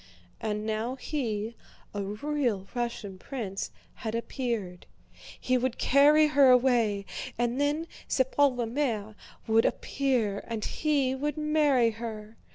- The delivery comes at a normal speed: No, slow, 125 wpm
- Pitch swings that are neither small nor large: Yes, average, 4.4 semitones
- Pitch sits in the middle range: No, high, 240 Hz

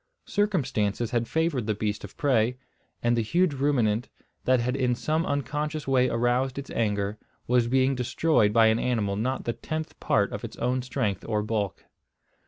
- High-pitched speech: No, low, 125 Hz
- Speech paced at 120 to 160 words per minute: No, average, 175 wpm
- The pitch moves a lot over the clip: No, average, 3.8 semitones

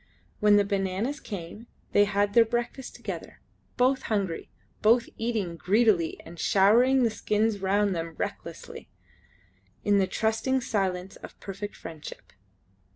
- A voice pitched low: No, high, 205 Hz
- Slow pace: Yes, slow, 130 wpm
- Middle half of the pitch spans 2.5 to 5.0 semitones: Yes, average, 3.2 semitones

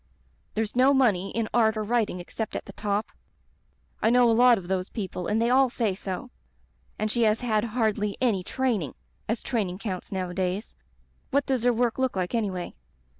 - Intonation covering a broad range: No, average, 3.9 semitones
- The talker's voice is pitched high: Yes, high, 220 Hz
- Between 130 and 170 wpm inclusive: No, average, 190 wpm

